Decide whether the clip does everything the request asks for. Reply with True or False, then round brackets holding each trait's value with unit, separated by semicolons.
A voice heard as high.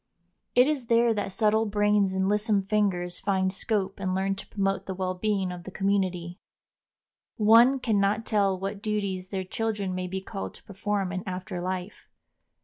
True (195 Hz)